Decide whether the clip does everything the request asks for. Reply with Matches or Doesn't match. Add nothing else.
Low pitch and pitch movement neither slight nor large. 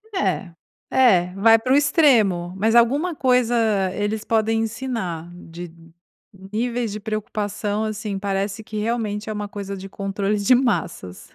Doesn't match